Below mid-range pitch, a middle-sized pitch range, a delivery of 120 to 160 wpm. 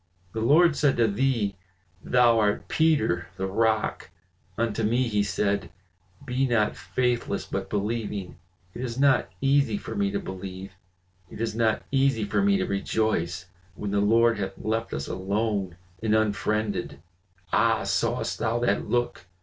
Yes: low, 110 Hz; average, 3.4 semitones; average, 150 wpm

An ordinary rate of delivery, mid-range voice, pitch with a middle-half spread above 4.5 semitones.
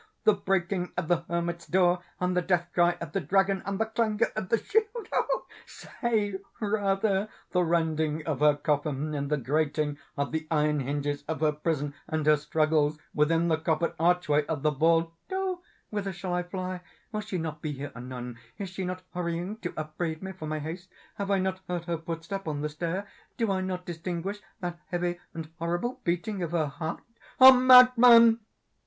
No: average, 185 wpm; medium, 175 Hz; average, 3.8 semitones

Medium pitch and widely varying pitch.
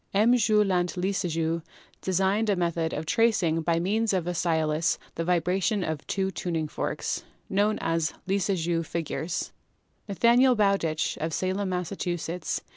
No: medium, 180 Hz; average, 3.3 semitones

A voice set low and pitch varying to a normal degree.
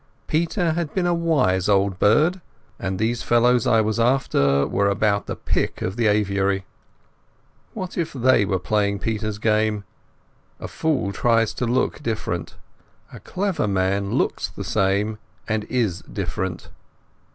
Yes: low, 110 Hz; average, 4.3 semitones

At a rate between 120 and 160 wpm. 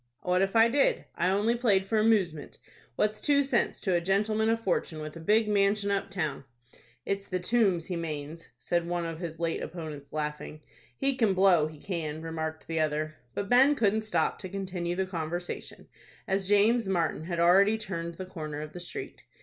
No: average, 190 wpm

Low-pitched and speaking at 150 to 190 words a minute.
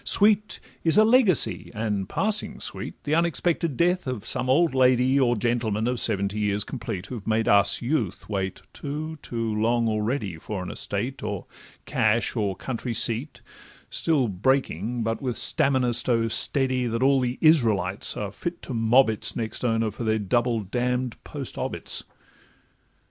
Yes: low, 120 Hz; average, 155 wpm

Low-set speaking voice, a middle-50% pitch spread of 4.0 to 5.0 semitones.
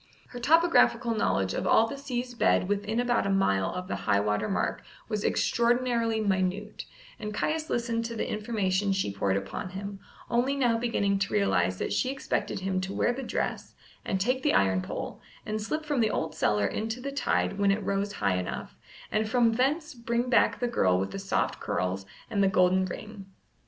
No: high, 210 Hz; average, 4.4 semitones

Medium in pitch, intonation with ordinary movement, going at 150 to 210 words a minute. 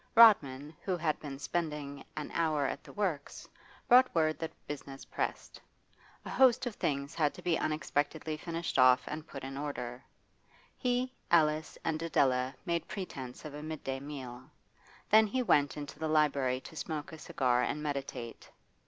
Yes: medium, 150 Hz; average, 3.2 semitones; average, 160 wpm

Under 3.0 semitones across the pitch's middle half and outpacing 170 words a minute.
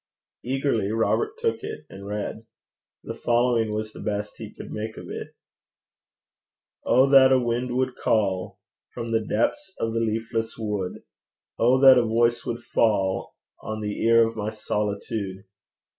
No: narrow, 2.5 semitones; average, 155 wpm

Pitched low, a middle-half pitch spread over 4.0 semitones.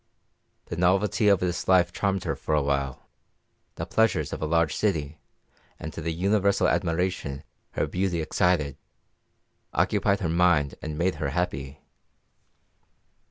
No: very low, 85 Hz; average, 3.5 semitones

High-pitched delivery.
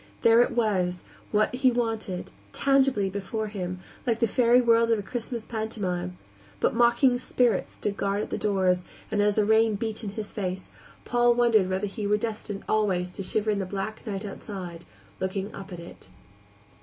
Yes: high, 210 Hz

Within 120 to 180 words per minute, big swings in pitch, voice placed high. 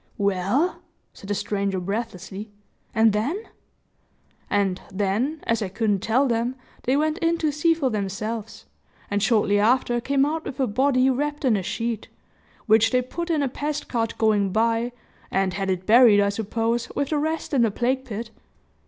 No: average, 175 wpm; average, 4.9 semitones; high, 230 Hz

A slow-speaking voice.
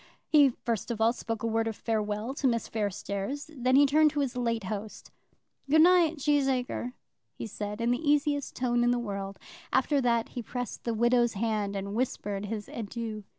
No: average, 190 wpm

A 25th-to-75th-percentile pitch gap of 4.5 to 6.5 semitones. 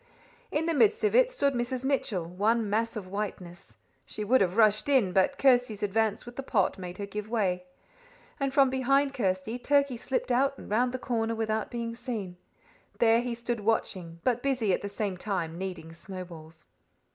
Yes: average, 5.0 semitones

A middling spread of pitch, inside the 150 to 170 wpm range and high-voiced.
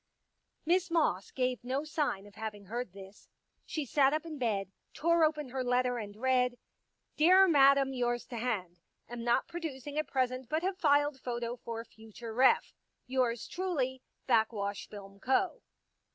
Yes: average, 4.4 semitones; average, 160 wpm; very high, 255 Hz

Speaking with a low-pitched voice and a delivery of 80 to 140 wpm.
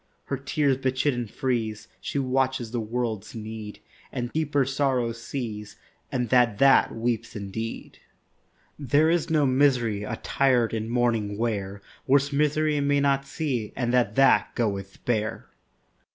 Yes: low, 125 Hz; slow, 135 wpm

